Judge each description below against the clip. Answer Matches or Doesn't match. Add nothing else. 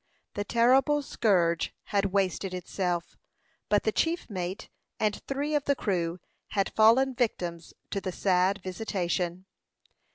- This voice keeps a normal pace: Doesn't match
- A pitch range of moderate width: Matches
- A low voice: Doesn't match